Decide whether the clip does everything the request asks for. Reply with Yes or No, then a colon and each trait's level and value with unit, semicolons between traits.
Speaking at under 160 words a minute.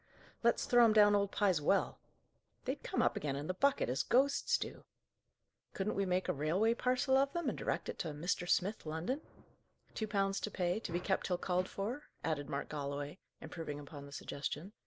No: average, 200 wpm